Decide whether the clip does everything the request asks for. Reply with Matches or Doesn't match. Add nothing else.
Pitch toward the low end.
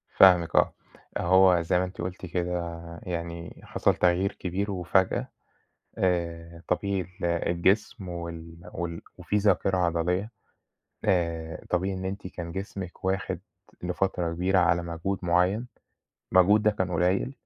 Matches